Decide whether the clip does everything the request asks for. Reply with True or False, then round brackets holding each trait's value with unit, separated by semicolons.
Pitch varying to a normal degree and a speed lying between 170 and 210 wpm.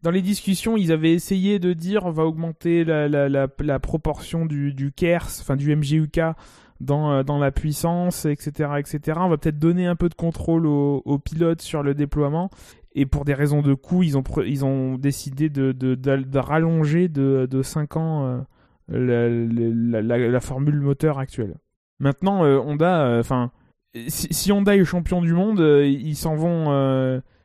True (3.5 semitones; 190 wpm)